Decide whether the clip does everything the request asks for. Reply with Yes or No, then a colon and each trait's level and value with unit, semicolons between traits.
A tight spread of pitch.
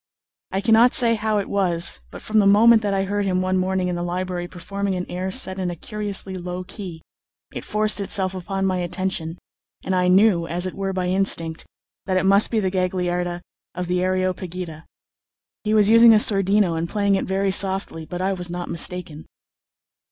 Yes: narrow, 2.0 semitones